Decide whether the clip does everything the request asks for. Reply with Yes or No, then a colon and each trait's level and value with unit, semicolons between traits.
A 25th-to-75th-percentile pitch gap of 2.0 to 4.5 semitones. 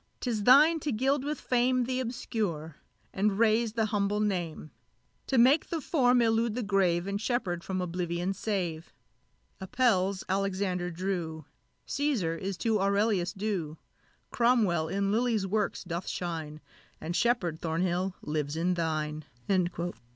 No: average, 5.2 semitones